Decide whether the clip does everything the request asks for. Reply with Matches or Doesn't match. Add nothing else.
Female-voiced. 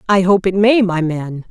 Matches